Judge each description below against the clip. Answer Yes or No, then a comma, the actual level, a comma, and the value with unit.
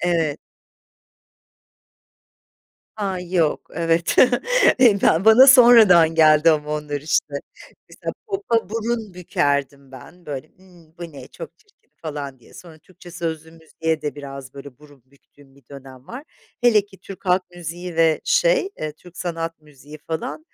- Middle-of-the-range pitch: Yes, medium, 165 Hz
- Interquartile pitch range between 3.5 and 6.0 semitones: Yes, average, 4.0 semitones